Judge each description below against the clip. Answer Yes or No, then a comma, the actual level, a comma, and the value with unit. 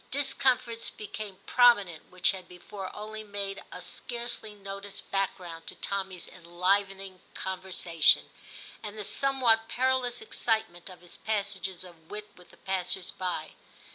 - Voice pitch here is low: No, high, 195 Hz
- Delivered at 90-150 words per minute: Yes, slow, 135 wpm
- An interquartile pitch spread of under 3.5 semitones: Yes, average, 3.1 semitones